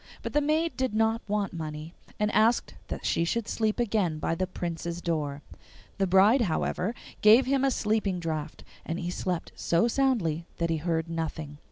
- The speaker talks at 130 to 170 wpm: No, average, 180 wpm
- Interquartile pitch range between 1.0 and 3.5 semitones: No, average, 5.3 semitones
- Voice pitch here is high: No, medium, 180 Hz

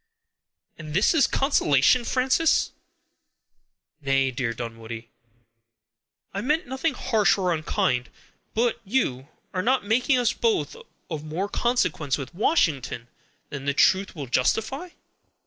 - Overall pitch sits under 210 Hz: Yes, medium, 185 Hz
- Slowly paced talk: Yes, slow, 120 wpm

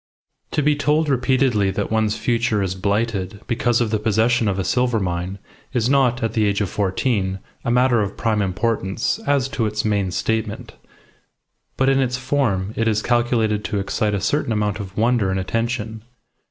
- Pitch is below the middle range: Yes, low, 110 Hz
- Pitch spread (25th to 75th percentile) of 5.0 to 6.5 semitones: No, average, 3.2 semitones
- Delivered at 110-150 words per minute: No, average, 180 wpm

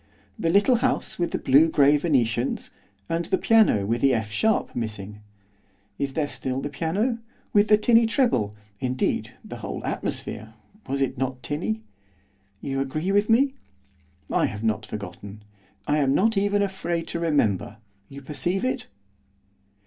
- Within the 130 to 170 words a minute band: Yes, average, 155 wpm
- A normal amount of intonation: No, wide, 8.7 semitones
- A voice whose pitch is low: No, medium, 145 Hz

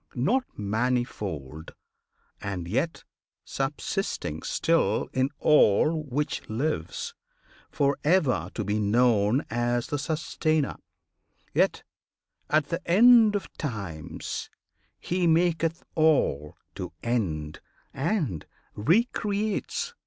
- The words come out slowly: Yes, slow, 95 wpm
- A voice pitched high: No, low, 135 Hz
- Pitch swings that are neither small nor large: No, wide, 8.2 semitones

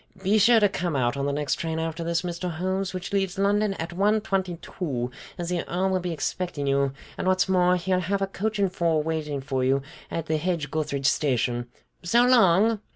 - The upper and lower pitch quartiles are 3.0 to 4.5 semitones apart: Yes, average, 4.1 semitones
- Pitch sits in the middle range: Yes, medium, 175 Hz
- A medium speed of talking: No, fast, 215 wpm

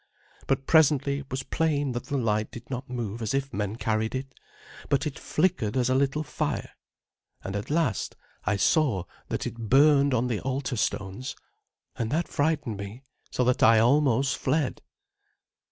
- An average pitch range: Yes, average, 4.0 semitones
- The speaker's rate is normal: Yes, average, 170 wpm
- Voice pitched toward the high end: No, low, 130 Hz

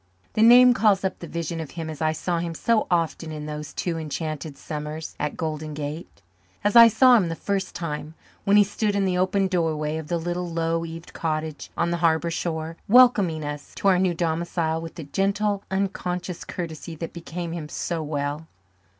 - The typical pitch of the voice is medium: Yes, medium, 165 Hz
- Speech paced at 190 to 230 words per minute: Yes, average, 195 wpm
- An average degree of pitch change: Yes, average, 3.0 semitones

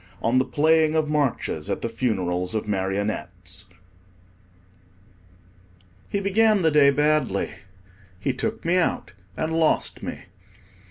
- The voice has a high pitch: No, medium, 140 Hz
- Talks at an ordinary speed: No, slow, 120 wpm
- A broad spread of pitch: Yes, wide, 7.8 semitones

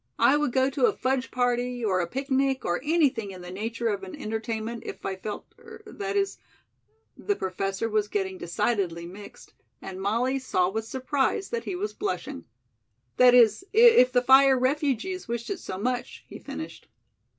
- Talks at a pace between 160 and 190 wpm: Yes, average, 180 wpm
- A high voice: Yes, high, 245 Hz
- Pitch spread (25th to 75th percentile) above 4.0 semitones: Yes, average, 5.0 semitones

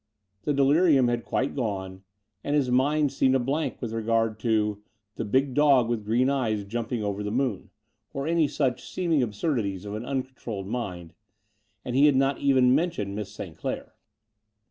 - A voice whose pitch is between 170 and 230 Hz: No, low, 125 Hz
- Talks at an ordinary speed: Yes, average, 170 wpm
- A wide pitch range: No, average, 4.5 semitones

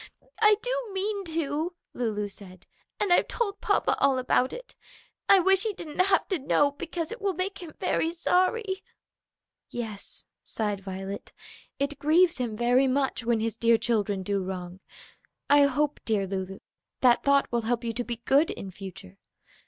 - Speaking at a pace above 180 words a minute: No, average, 170 wpm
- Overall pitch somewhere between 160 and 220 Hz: No, very high, 265 Hz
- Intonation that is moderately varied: No, wide, 8.6 semitones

